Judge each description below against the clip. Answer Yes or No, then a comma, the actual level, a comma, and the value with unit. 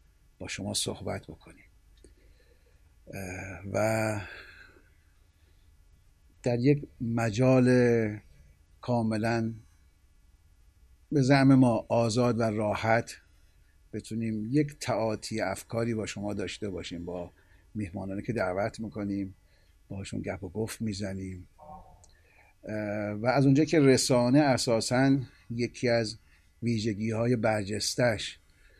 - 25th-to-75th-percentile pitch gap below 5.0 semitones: No, wide, 5.4 semitones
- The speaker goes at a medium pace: No, slow, 95 wpm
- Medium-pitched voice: No, low, 105 Hz